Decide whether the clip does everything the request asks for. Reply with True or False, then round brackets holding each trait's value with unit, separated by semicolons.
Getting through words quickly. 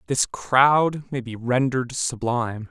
False (135 wpm)